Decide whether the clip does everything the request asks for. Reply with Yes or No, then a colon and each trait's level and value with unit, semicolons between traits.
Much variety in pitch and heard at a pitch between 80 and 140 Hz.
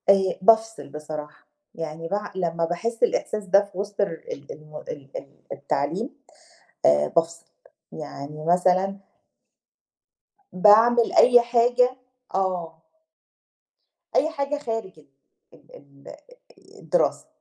No: wide, 5.8 semitones; medium, 185 Hz